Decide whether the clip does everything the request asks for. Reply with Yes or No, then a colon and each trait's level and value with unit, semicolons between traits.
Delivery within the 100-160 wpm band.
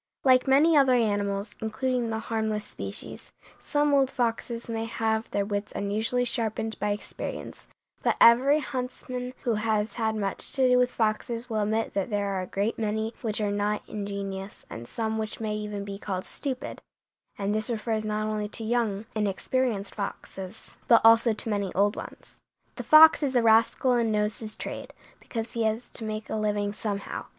No: average, 180 wpm